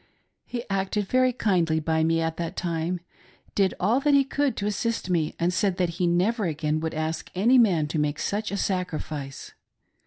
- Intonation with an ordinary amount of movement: Yes, average, 4.4 semitones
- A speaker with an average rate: Yes, average, 190 wpm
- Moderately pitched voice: Yes, medium, 180 Hz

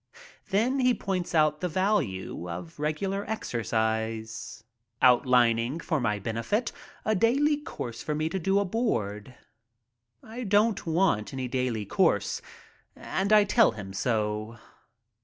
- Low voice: No, medium, 150 Hz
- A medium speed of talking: No, slow, 125 wpm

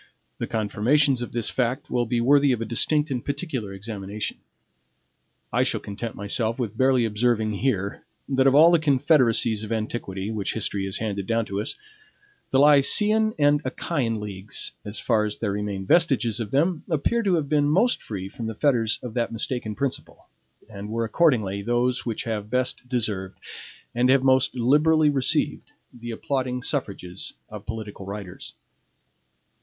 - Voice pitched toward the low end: Yes, low, 120 Hz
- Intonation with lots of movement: No, average, 4.6 semitones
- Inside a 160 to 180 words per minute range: Yes, average, 165 wpm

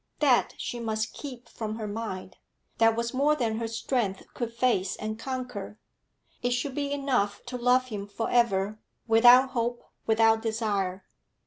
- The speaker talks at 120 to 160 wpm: Yes, average, 155 wpm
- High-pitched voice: Yes, high, 230 Hz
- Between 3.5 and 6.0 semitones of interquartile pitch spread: No, narrow, 2.5 semitones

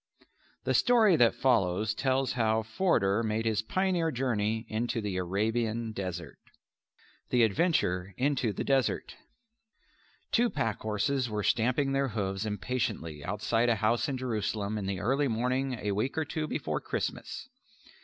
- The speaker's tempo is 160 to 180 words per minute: No, average, 145 wpm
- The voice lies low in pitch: Yes, low, 115 Hz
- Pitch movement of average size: Yes, average, 4.0 semitones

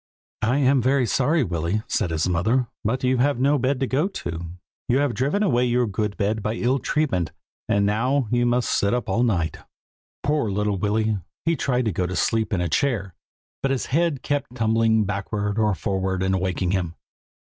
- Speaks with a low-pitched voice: Yes, low, 115 Hz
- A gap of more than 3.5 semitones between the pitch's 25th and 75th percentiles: Yes, average, 4.8 semitones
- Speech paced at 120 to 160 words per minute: No, average, 195 wpm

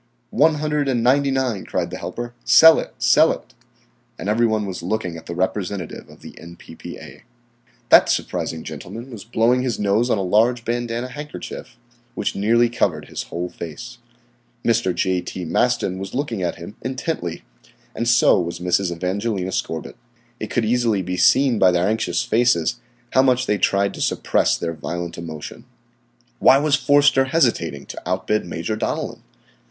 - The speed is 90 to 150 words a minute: No, average, 165 wpm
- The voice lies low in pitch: Yes, low, 110 Hz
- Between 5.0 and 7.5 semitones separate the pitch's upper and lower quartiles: Yes, wide, 5.4 semitones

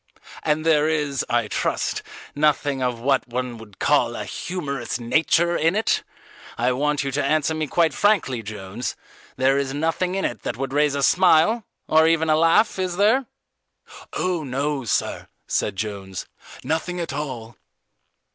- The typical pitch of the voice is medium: Yes, medium, 145 Hz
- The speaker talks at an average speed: Yes, average, 160 wpm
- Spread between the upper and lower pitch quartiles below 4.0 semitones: No, average, 4.5 semitones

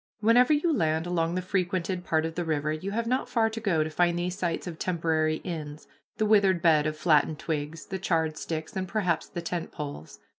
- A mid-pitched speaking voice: Yes, medium, 170 Hz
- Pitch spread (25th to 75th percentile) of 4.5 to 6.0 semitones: No, average, 3.3 semitones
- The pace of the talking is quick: Yes, fast, 215 wpm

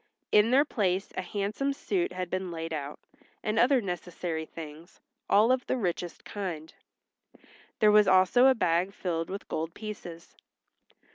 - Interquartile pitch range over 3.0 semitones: Yes, average, 4.2 semitones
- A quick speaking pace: No, average, 150 wpm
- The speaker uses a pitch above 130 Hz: Yes, medium, 185 Hz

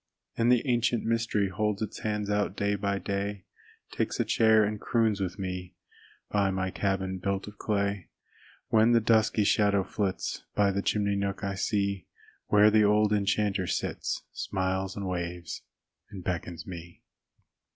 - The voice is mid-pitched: No, low, 100 Hz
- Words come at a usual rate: Yes, average, 155 wpm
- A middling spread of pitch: No, narrow, 1.9 semitones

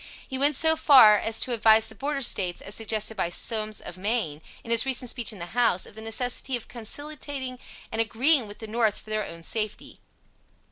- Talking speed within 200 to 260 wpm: Yes, fast, 205 wpm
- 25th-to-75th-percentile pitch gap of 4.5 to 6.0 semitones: No, average, 3.1 semitones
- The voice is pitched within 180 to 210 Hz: No, high, 225 Hz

